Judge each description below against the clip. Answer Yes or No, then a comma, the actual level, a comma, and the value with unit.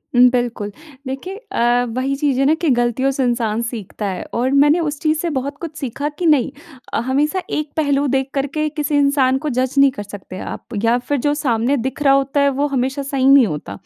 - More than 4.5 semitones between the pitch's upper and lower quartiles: No, average, 3.0 semitones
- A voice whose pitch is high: Yes, very high, 275 Hz